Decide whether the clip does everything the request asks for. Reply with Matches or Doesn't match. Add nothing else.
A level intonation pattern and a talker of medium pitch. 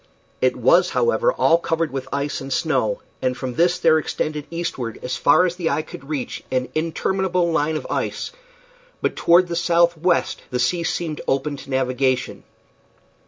Doesn't match